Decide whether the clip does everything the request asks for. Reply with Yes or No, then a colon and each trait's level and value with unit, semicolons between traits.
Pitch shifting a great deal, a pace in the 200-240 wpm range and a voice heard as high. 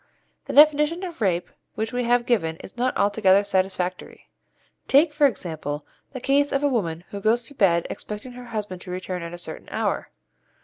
No: wide, 6.0 semitones; average, 185 wpm; high, 215 Hz